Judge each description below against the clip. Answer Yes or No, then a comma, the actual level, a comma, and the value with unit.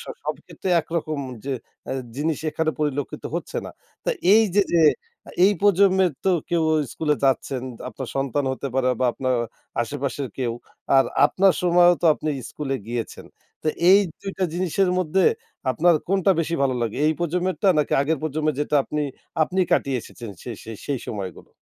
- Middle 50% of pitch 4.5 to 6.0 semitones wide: Yes, average, 5.0 semitones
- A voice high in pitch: No, medium, 155 Hz